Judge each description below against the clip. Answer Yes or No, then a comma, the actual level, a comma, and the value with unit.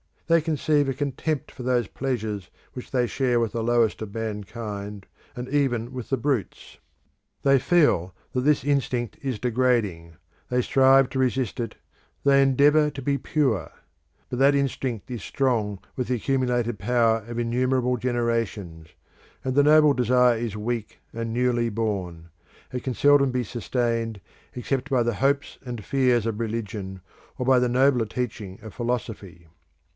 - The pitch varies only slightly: No, average, 3.0 semitones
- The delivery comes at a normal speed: Yes, average, 155 wpm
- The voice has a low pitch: Yes, low, 125 Hz